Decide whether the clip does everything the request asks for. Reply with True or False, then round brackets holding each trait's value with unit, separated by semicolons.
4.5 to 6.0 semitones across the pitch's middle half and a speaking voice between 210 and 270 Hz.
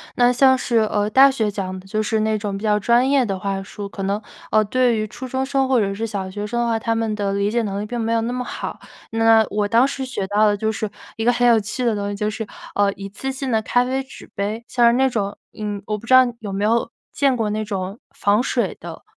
False (3.0 semitones; 220 Hz)